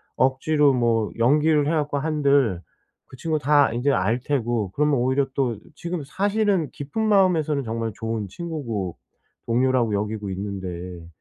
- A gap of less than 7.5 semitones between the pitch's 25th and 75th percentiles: Yes, average, 5.1 semitones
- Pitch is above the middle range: No, low, 130 Hz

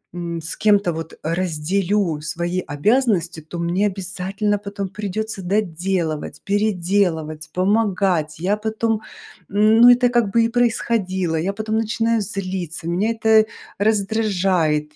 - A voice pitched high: Yes, high, 195 Hz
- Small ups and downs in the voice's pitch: No, average, 4.0 semitones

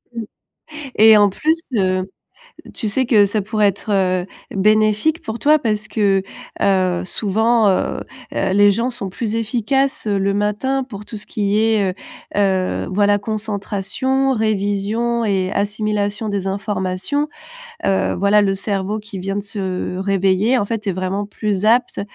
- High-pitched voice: Yes, high, 205 Hz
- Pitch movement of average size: No, narrow, 2.2 semitones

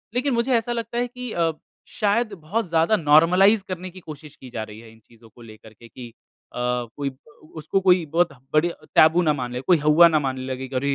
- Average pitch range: No, wide, 6.7 semitones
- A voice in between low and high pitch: Yes, medium, 155 Hz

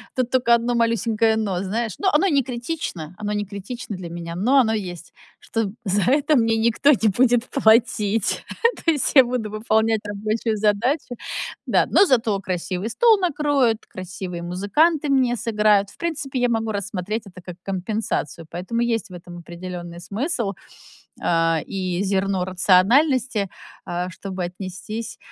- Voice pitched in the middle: No, high, 215 Hz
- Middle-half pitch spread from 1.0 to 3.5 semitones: No, average, 4.6 semitones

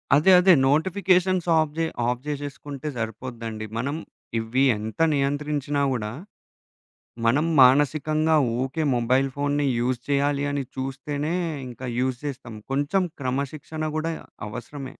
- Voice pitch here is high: No, medium, 140 Hz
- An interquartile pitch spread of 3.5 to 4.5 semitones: No, average, 3.0 semitones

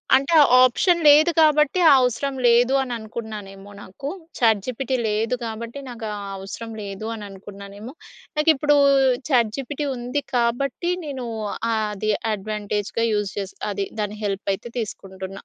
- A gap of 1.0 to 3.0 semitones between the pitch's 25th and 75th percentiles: No, average, 4.5 semitones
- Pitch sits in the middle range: No, high, 230 Hz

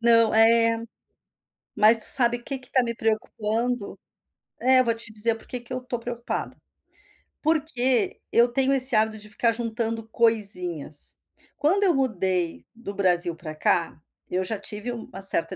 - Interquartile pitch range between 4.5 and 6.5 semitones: No, average, 2.8 semitones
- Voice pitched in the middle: No, high, 230 Hz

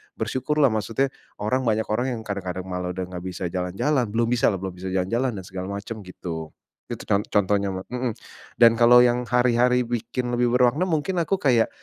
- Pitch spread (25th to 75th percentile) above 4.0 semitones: Yes, average, 4.7 semitones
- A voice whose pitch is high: No, low, 115 Hz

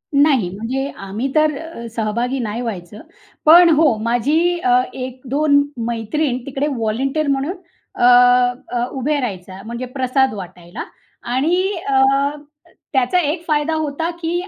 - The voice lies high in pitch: Yes, very high, 265 Hz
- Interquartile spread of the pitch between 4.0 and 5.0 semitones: Yes, average, 4.6 semitones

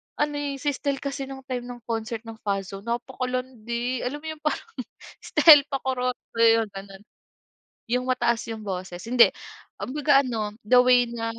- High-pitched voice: Yes, very high, 250 Hz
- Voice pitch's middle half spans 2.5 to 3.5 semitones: Yes, average, 3.0 semitones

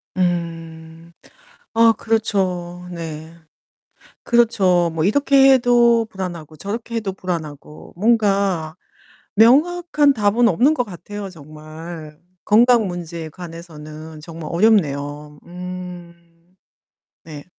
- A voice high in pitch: No, medium, 180 Hz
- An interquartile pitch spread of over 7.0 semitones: No, wide, 5.4 semitones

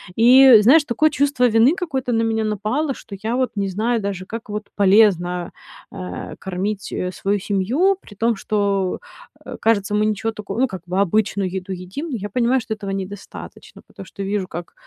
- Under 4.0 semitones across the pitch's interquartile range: Yes, average, 3.6 semitones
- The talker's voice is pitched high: Yes, high, 210 Hz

